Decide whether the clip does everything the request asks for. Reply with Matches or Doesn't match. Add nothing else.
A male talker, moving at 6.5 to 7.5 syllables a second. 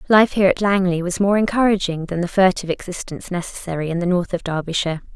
Doesn't match